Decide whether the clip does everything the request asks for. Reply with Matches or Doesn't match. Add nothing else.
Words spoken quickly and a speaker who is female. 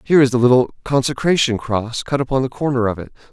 Doesn't match